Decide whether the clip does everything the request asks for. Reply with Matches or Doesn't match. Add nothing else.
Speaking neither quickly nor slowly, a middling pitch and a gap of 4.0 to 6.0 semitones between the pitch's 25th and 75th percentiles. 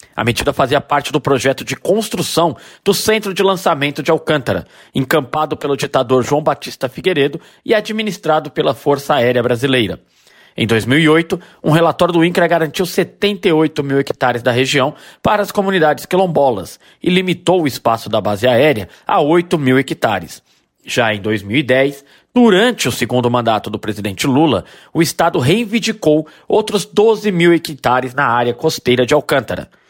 Matches